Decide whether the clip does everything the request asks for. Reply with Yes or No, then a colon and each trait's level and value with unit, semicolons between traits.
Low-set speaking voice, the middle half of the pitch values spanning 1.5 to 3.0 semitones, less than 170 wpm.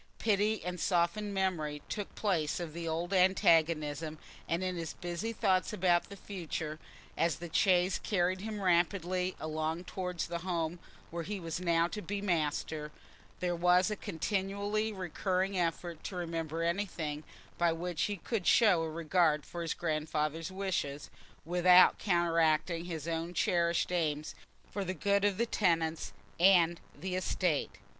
No: medium, 175 Hz; narrow, 2.5 semitones; average, 150 wpm